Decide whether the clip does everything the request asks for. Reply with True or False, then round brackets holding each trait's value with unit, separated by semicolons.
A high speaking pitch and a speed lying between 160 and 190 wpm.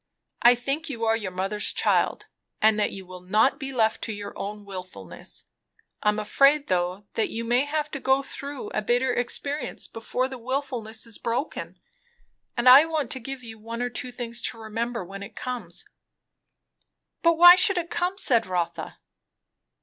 True (235 Hz; 180 wpm)